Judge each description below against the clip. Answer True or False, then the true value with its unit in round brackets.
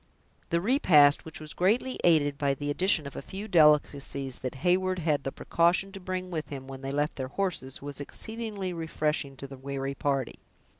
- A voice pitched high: False (150 Hz)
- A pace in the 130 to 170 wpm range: False (190 wpm)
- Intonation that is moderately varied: True (4.8 semitones)